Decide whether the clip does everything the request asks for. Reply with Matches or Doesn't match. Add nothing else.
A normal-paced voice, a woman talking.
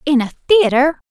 Matches